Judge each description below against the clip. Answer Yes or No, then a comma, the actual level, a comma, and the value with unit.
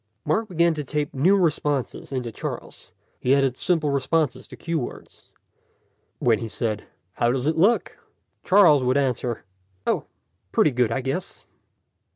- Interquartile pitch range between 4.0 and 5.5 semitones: Yes, average, 4.6 semitones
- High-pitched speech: No, medium, 140 Hz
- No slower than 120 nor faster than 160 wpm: Yes, average, 150 wpm